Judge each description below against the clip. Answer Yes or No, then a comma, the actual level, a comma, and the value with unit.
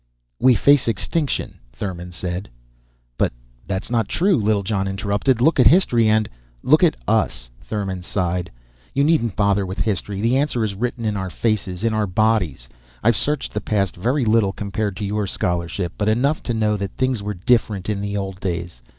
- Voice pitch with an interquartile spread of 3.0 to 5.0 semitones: Yes, average, 3.4 semitones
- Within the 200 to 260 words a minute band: No, average, 185 wpm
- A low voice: Yes, low, 105 Hz